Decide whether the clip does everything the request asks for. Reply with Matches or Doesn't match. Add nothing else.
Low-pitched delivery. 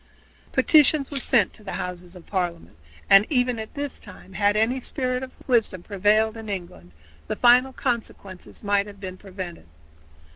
Doesn't match